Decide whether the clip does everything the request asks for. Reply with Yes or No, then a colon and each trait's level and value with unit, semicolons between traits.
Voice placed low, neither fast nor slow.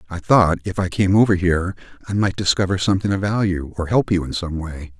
No: very low, 90 Hz; fast, 230 wpm